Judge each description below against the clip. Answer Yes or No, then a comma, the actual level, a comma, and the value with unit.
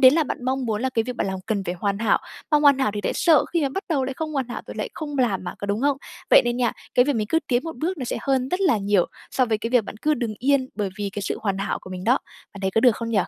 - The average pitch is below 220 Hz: No, high, 245 Hz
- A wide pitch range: No, average, 5.0 semitones